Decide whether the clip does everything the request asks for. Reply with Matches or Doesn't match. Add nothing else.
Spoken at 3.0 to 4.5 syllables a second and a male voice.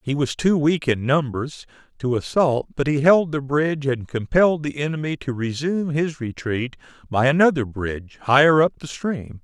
Doesn't match